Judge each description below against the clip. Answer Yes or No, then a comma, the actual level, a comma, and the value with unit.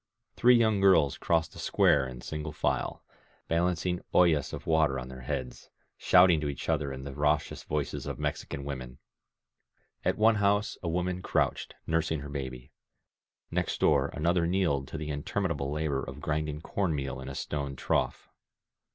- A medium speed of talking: Yes, average, 170 wpm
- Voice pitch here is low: Yes, very low, 75 Hz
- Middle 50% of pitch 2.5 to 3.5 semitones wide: No, average, 4.0 semitones